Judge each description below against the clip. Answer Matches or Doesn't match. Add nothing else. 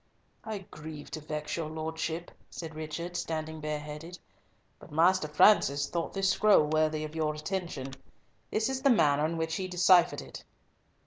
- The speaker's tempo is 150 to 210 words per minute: Matches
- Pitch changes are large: Doesn't match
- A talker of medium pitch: Matches